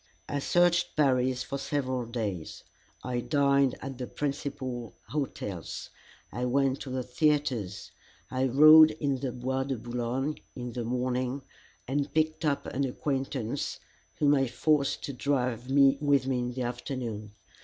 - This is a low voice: Yes, low, 130 Hz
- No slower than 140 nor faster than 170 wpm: Yes, average, 145 wpm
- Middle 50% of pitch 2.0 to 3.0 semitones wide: Yes, narrow, 2.4 semitones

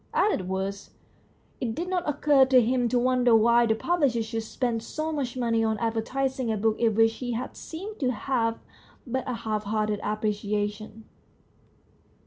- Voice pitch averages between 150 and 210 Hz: No, high, 230 Hz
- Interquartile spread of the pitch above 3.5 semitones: No, average, 2.9 semitones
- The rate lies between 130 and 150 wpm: No, average, 170 wpm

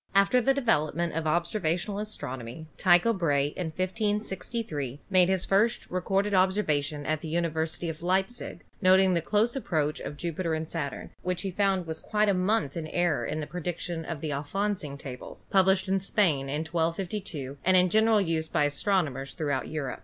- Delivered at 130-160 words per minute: No, average, 175 wpm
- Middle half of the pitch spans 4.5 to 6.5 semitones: No, average, 4.0 semitones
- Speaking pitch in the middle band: Yes, medium, 175 Hz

